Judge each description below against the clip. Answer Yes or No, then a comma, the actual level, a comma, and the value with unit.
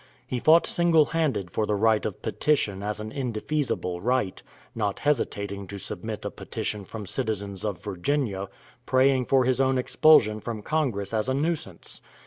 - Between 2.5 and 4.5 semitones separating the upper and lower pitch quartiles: No, average, 5.1 semitones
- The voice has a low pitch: Yes, low, 110 Hz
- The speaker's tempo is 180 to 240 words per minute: No, average, 160 wpm